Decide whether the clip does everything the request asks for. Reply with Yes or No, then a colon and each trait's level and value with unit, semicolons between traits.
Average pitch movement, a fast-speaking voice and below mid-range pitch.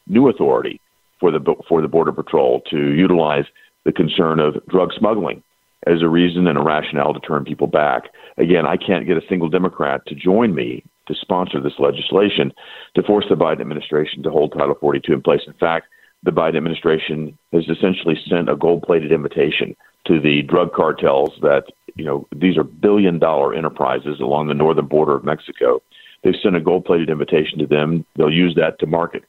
No: average, 3.4 semitones; average, 190 wpm; very low, 80 Hz